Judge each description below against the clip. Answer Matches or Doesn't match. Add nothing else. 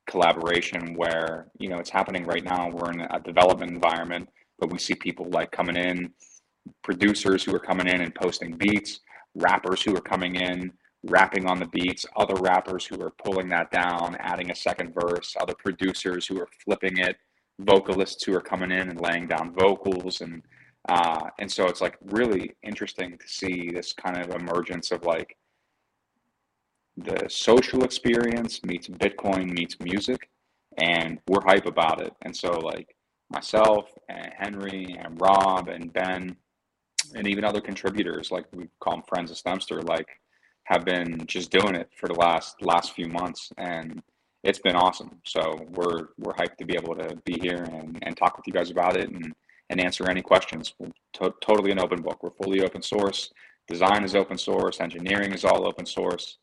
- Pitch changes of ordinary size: Doesn't match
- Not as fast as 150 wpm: Doesn't match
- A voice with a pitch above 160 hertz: Doesn't match